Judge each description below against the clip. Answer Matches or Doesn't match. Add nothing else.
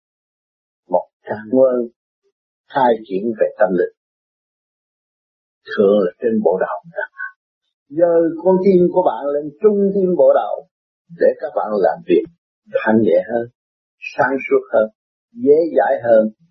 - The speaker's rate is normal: Doesn't match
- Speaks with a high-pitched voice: Matches